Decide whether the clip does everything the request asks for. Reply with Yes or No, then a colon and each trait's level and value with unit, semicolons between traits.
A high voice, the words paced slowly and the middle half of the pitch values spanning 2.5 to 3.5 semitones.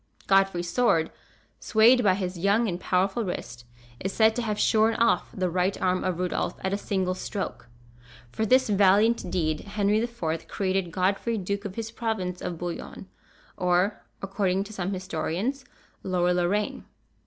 No: high, 195 Hz; average, 155 wpm; average, 3.1 semitones